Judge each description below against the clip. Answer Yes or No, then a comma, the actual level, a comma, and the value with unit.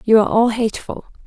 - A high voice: Yes, high, 225 Hz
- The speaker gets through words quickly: No, average, 145 wpm